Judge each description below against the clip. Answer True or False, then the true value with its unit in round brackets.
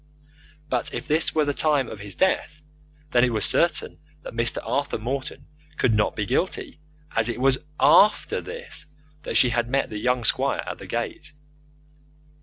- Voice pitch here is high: False (130 Hz)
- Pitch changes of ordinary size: True (4.5 semitones)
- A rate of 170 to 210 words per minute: True (175 wpm)